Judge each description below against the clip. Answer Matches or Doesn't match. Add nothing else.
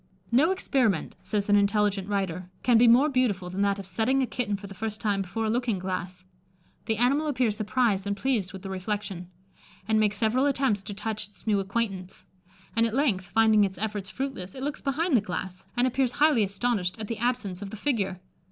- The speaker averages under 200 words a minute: Doesn't match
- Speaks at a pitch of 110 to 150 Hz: Doesn't match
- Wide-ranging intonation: Doesn't match